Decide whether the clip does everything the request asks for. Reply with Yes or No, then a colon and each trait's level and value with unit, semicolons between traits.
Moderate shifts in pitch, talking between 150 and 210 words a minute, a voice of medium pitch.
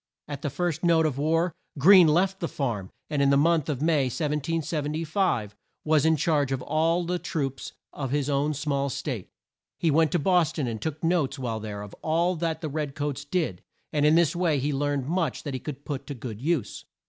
Yes: average, 3.0 semitones; fast, 205 wpm; medium, 150 Hz